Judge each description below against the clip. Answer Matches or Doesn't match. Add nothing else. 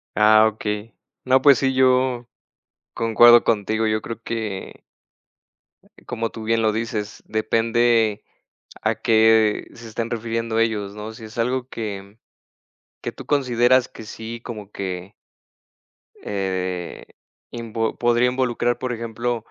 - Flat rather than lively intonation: Matches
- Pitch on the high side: Doesn't match